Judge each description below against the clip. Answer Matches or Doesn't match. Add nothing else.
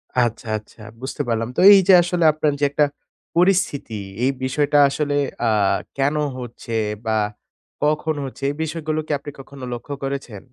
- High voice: Doesn't match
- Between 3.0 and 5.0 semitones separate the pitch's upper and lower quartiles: Matches